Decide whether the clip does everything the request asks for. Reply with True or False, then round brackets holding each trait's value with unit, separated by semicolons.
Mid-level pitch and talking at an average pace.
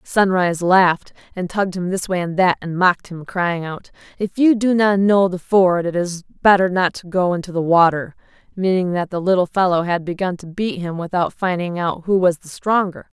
False (180 Hz; 215 wpm)